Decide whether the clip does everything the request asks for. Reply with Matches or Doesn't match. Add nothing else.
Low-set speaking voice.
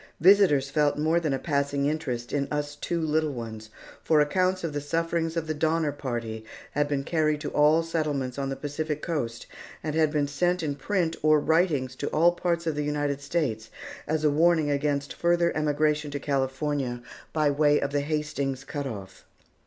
Doesn't match